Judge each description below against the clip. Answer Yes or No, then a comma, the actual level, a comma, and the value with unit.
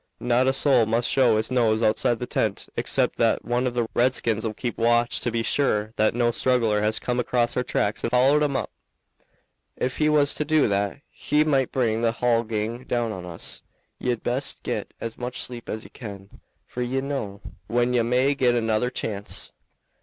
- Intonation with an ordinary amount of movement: No, narrow, 2.3 semitones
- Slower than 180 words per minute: No, average, 200 wpm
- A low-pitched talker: Yes, low, 120 Hz